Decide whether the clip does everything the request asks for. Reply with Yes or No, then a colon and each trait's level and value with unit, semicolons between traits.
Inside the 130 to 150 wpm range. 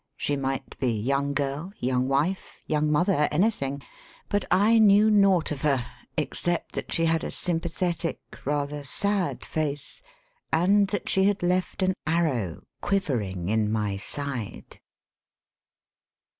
Yes: average, 140 wpm